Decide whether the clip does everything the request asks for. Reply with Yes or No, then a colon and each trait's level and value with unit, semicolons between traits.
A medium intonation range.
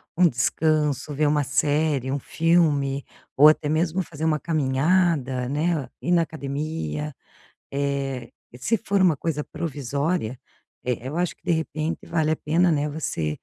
Yes: average, 3.1 semitones